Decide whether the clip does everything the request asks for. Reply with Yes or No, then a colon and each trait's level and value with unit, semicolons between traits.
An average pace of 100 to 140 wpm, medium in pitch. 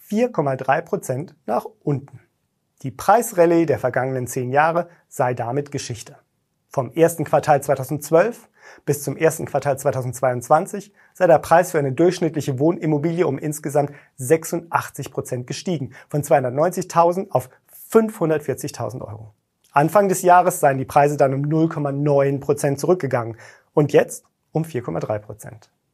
Yes: slow, 125 wpm; medium, 145 Hz